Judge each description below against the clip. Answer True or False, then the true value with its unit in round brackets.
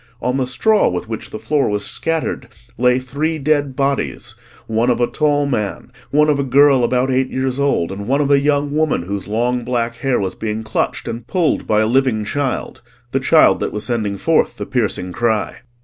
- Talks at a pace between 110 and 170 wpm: False (200 wpm)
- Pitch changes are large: False (4.3 semitones)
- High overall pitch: False (125 Hz)